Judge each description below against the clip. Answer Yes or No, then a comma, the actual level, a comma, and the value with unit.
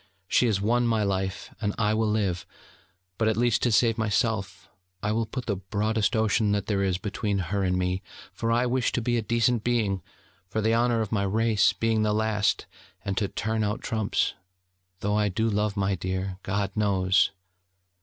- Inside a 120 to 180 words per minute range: No, average, 195 wpm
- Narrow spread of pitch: Yes, narrow, 2.3 semitones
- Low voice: Yes, low, 105 Hz